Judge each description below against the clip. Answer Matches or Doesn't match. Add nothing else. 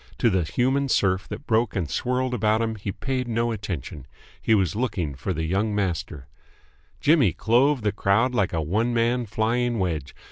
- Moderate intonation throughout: Matches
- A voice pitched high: Doesn't match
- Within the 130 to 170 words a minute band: Doesn't match